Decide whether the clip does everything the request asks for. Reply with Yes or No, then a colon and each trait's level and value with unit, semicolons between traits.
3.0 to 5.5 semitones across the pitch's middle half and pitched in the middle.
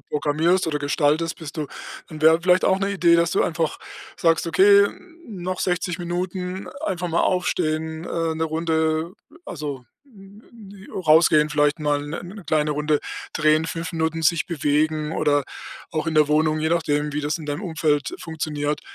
No: narrow, 2.4 semitones; medium, 160 Hz